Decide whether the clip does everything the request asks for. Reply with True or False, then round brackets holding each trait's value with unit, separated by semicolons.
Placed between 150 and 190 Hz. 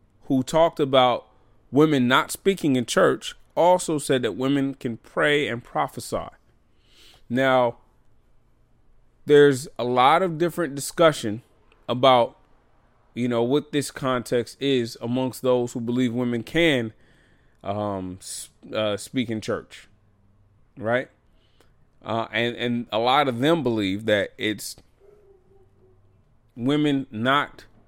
False (120 Hz)